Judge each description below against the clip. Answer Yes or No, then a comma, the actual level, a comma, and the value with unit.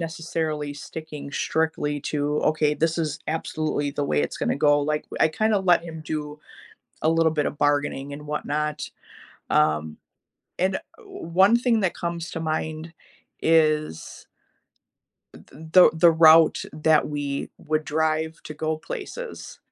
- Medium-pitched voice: Yes, medium, 155 Hz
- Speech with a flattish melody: Yes, narrow, 1.8 semitones